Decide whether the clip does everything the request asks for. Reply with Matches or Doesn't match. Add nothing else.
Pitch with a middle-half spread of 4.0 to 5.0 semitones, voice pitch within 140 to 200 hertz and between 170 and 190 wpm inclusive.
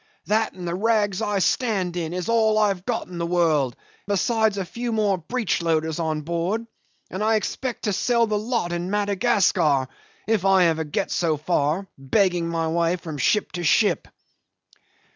Matches